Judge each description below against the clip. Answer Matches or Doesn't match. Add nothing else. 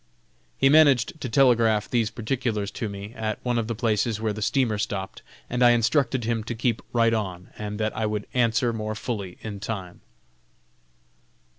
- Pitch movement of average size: Doesn't match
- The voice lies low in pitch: Matches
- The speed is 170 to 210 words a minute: Matches